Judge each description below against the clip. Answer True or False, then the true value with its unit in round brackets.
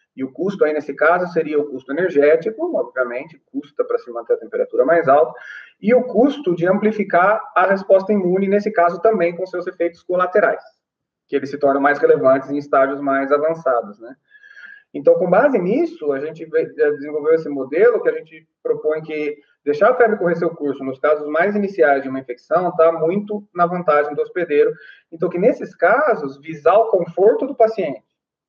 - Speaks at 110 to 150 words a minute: False (185 wpm)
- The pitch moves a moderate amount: False (7.6 semitones)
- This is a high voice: False (180 Hz)